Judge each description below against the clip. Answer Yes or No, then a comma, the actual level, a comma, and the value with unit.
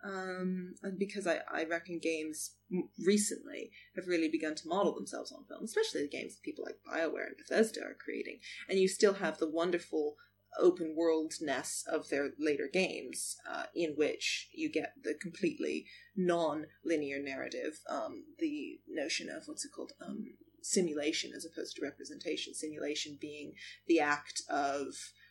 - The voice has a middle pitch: Yes, medium, 175 Hz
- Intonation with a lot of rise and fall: Yes, wide, 5.9 semitones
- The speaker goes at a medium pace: Yes, average, 160 wpm